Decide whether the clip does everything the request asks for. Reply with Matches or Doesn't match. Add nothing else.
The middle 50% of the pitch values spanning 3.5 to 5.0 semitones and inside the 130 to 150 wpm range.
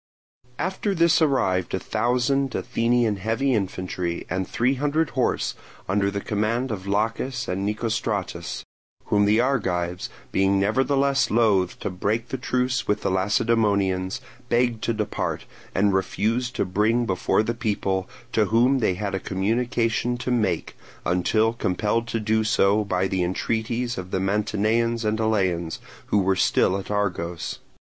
Matches